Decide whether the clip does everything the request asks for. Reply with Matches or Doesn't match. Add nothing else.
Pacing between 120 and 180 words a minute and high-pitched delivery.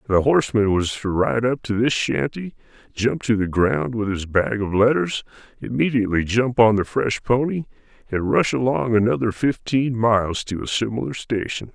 Doesn't match